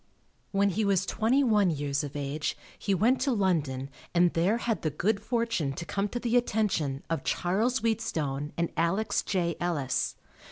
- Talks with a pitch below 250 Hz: Yes, medium, 185 Hz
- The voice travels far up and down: Yes, wide, 6.4 semitones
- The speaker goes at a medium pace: Yes, average, 170 wpm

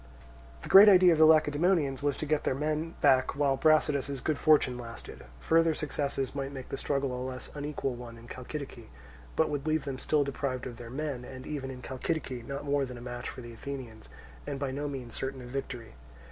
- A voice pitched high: No, medium, 140 Hz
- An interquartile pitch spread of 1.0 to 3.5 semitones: Yes, average, 2.9 semitones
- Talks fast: Yes, fast, 210 wpm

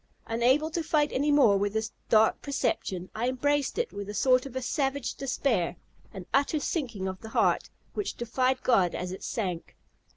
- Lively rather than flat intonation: Yes, wide, 5.7 semitones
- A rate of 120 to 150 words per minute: No, average, 175 wpm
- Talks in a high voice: Yes, very high, 250 Hz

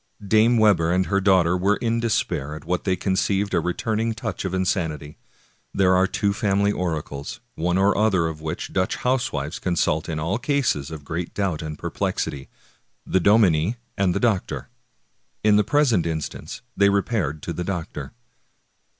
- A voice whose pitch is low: Yes, very low, 95 Hz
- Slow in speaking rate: No, average, 170 wpm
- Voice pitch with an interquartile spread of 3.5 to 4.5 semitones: Yes, average, 4.2 semitones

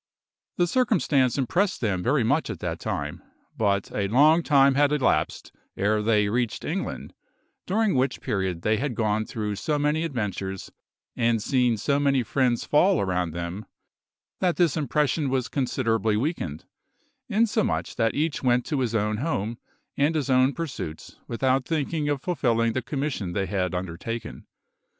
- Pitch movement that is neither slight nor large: No, wide, 5.7 semitones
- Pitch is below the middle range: Yes, low, 125 Hz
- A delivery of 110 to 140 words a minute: No, average, 155 wpm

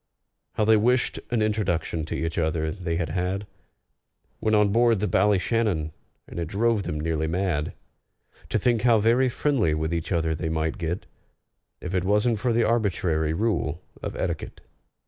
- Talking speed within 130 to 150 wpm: No, average, 165 wpm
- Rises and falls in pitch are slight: No, wide, 5.4 semitones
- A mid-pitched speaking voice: No, very low, 95 Hz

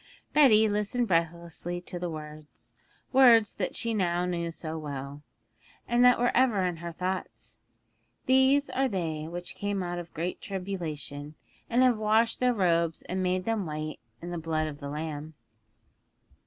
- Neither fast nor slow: Yes, average, 160 wpm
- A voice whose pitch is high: No, medium, 180 Hz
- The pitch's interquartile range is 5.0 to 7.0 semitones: Yes, average, 5.3 semitones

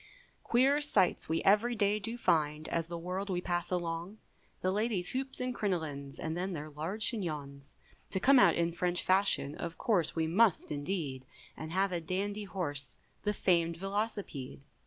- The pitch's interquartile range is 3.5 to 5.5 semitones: Yes, average, 4.2 semitones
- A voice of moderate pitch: Yes, medium, 180 Hz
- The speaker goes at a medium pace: Yes, average, 170 wpm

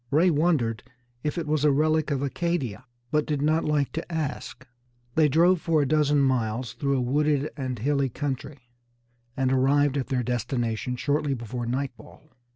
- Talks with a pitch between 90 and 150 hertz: Yes, medium, 140 Hz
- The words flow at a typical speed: Yes, average, 165 wpm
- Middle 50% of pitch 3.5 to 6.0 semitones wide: No, average, 3.0 semitones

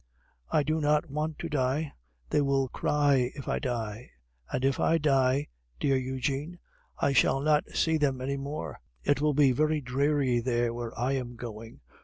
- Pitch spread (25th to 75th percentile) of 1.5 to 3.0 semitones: Yes, average, 2.7 semitones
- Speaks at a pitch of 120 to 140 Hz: Yes, low, 135 Hz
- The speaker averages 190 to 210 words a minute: No, average, 175 wpm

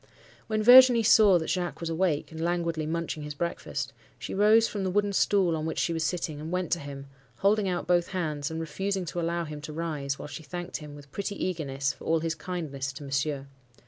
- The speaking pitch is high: No, medium, 165 Hz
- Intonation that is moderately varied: Yes, average, 3.6 semitones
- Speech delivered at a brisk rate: Yes, fast, 220 wpm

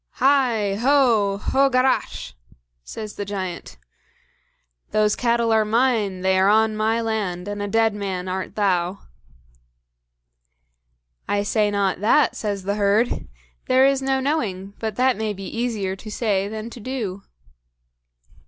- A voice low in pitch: No, high, 215 Hz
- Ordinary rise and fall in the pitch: Yes, average, 3.1 semitones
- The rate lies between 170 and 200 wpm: No, average, 140 wpm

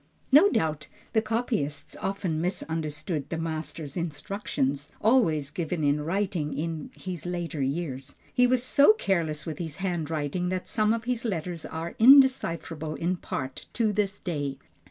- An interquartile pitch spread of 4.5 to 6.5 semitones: Yes, average, 4.8 semitones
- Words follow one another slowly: No, average, 145 wpm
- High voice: No, medium, 170 Hz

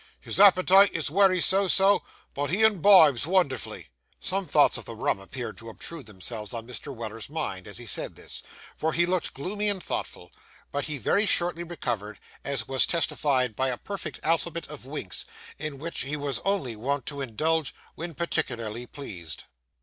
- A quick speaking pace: No, average, 175 wpm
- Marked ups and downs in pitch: Yes, wide, 6.3 semitones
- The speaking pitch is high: No, medium, 145 Hz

